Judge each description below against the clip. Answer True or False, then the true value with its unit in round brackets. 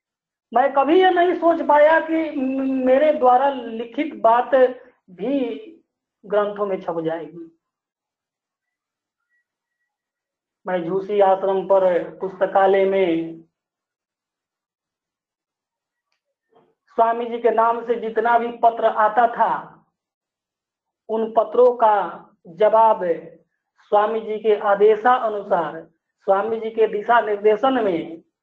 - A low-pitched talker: False (225 Hz)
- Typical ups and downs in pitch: True (4.6 semitones)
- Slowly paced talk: True (100 wpm)